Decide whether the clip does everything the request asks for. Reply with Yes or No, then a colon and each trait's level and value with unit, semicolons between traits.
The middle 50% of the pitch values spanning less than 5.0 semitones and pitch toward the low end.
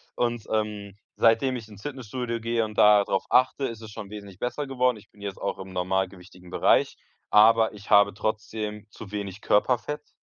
Yes: narrow, 2.6 semitones; low, 105 Hz